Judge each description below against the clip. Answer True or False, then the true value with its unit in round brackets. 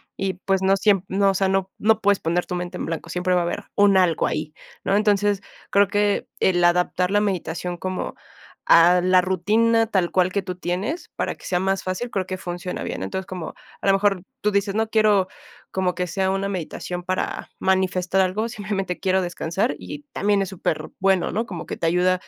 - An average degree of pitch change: False (2.1 semitones)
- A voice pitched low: False (190 Hz)